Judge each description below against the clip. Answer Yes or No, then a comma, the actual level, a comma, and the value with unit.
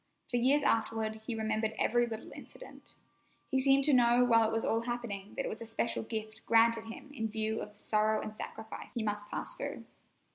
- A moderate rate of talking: No, fast, 210 wpm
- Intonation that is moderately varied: No, narrow, 1.7 semitones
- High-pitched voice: Yes, high, 225 Hz